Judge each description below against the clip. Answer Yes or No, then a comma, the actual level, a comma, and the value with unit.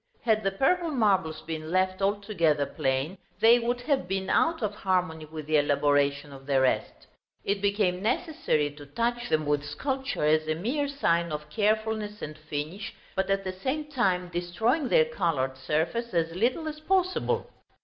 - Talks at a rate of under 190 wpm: Yes, average, 170 wpm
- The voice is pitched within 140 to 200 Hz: Yes, high, 190 Hz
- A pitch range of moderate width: No, wide, 7.2 semitones